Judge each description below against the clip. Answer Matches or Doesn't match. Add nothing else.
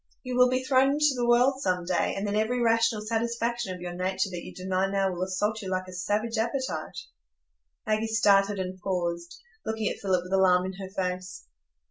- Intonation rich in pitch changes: Doesn't match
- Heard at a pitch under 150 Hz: Doesn't match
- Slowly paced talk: Doesn't match